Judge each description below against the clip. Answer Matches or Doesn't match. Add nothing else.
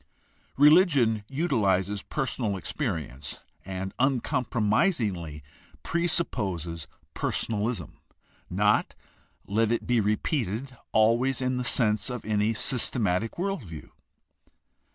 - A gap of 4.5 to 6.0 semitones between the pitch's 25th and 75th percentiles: Matches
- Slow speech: Matches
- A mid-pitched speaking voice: Doesn't match